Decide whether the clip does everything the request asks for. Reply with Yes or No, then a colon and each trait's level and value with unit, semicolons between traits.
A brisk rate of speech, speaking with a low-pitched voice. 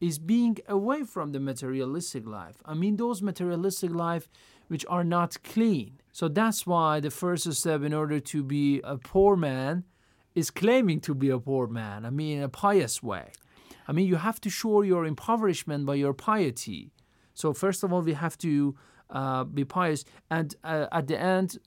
No: fast, 190 wpm; medium, 160 Hz